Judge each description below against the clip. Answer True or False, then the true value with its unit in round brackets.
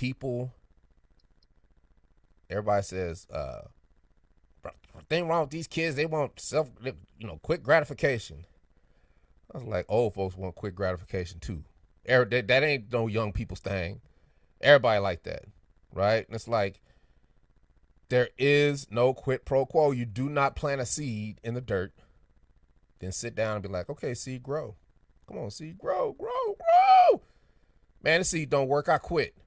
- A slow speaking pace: False (155 wpm)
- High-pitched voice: False (110 Hz)